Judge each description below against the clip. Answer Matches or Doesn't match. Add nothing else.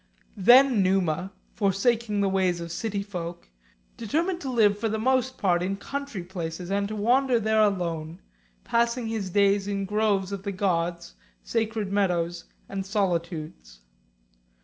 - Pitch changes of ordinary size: Matches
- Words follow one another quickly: Doesn't match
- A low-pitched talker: Doesn't match